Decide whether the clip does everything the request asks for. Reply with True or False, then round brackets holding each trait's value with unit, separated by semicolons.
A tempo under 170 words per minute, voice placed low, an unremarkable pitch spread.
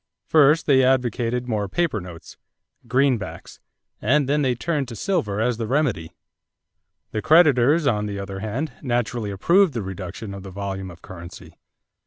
False (155 wpm; 120 Hz; 6.0 semitones)